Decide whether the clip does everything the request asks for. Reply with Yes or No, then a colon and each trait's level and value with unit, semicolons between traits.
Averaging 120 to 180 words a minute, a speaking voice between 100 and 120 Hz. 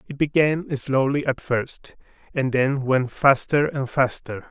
No: average, 145 wpm; low, 135 Hz